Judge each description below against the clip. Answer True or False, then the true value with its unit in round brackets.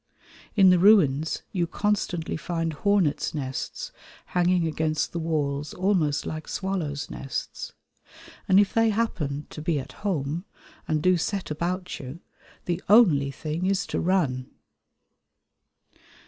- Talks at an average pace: False (130 wpm)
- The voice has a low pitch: False (170 Hz)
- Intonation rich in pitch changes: False (4.0 semitones)